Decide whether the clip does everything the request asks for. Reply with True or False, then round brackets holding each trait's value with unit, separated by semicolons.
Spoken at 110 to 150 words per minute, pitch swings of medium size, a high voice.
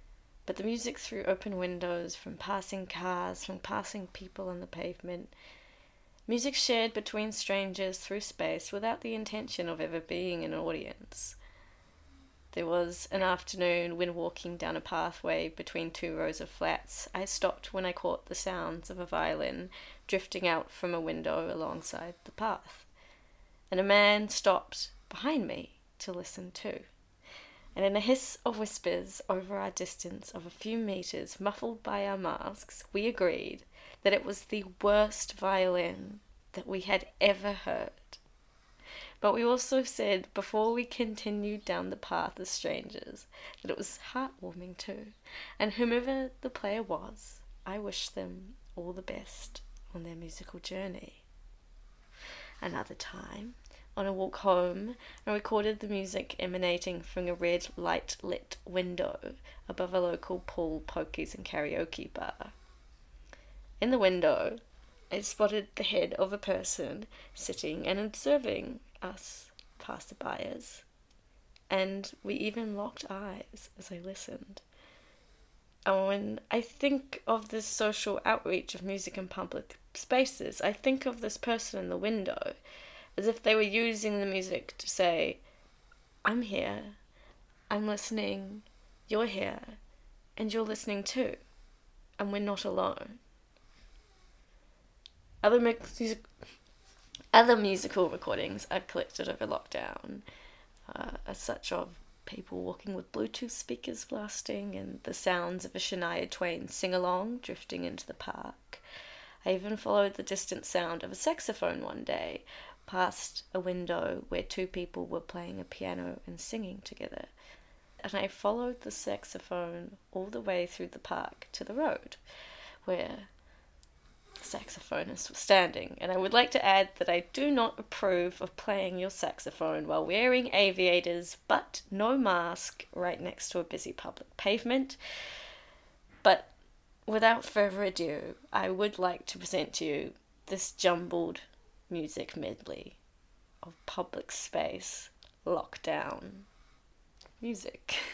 True (140 wpm; 3.5 semitones; 195 Hz)